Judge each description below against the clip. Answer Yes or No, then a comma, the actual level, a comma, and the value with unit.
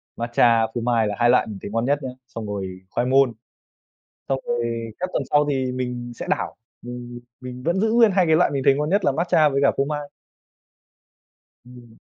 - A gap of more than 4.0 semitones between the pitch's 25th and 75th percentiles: No, average, 3.6 semitones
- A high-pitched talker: No, low, 125 Hz